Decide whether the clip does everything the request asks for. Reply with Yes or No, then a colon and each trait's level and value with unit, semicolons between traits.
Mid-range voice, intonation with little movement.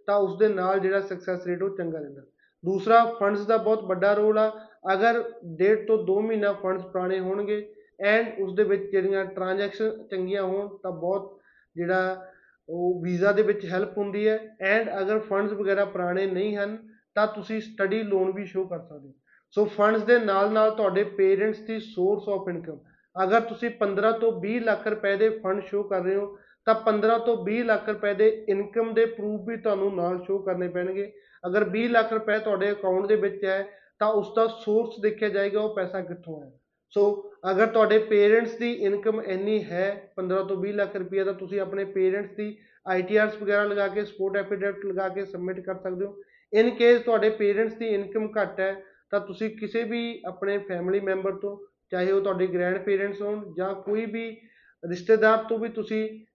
No: high, 200 Hz; narrow, 2.1 semitones